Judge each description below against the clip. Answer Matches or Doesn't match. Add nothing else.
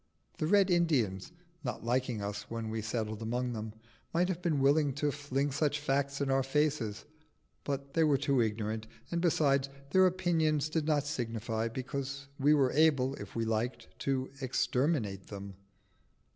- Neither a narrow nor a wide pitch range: Matches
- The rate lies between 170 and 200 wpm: Doesn't match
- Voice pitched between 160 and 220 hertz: Doesn't match